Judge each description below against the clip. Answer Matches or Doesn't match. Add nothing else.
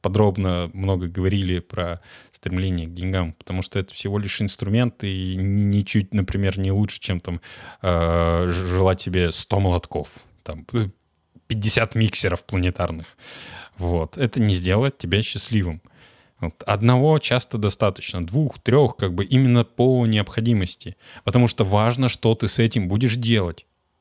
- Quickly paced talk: Doesn't match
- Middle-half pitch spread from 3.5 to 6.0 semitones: Matches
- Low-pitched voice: Matches